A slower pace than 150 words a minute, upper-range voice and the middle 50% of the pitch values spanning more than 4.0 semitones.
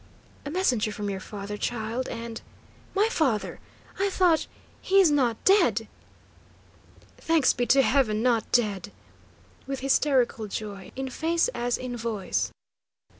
Yes: average, 140 wpm; high, 245 Hz; wide, 5.5 semitones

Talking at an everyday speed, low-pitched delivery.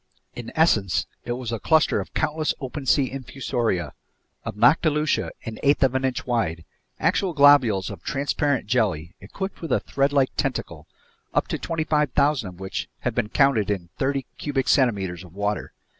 Yes: average, 160 wpm; low, 130 Hz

